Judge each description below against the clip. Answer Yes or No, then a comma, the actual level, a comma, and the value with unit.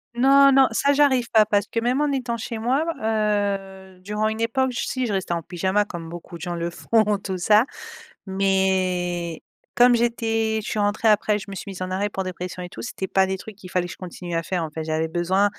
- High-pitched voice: Yes, high, 200 Hz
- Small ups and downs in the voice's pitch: No, average, 3.6 semitones